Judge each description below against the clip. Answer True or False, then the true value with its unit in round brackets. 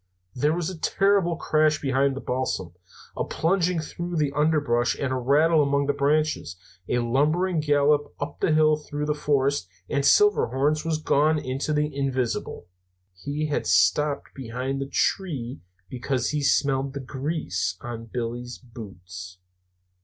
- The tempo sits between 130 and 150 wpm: True (145 wpm)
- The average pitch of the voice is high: False (140 Hz)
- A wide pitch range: False (3.3 semitones)